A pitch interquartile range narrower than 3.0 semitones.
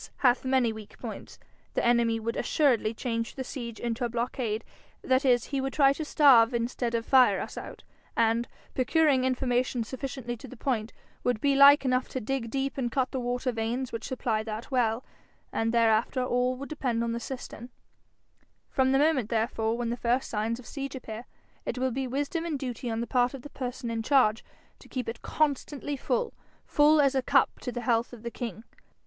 Yes: narrow, 2.6 semitones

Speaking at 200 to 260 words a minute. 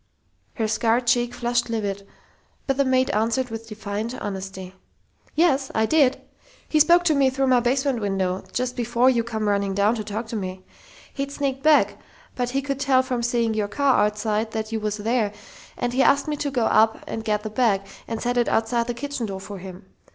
Yes: fast, 205 wpm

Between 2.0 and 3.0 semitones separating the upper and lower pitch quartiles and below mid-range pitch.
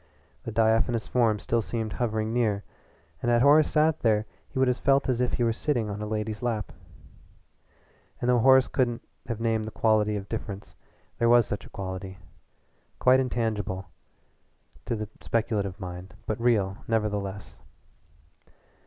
Yes: narrow, 2.5 semitones; low, 110 Hz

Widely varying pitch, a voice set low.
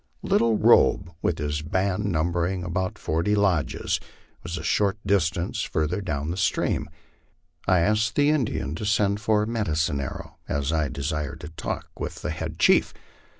No: average, 4.6 semitones; very low, 90 Hz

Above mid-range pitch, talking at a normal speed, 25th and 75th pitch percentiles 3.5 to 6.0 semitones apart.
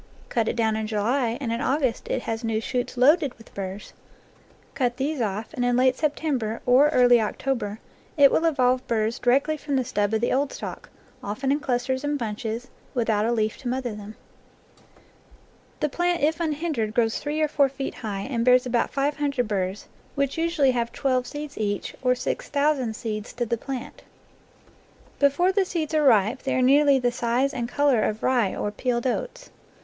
Yes: very high, 250 Hz; average, 195 wpm; average, 3.9 semitones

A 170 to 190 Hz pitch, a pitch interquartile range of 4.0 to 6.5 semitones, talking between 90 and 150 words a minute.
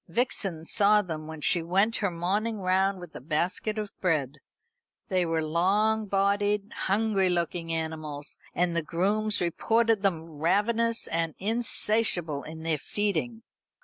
Yes: medium, 185 Hz; average, 4.3 semitones; average, 140 wpm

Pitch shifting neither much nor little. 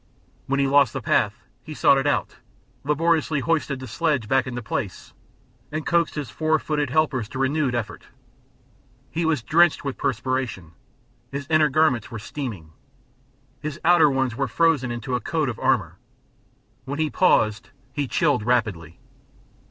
Yes: average, 4.2 semitones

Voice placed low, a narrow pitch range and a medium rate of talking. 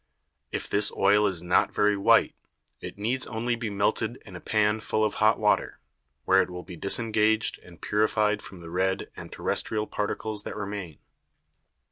Yes: low, 105 Hz; narrow, 2.1 semitones; average, 170 wpm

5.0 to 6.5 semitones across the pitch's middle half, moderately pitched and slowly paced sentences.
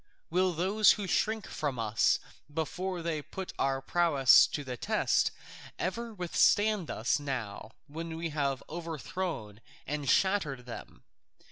Yes: wide, 5.5 semitones; medium, 160 Hz; slow, 130 wpm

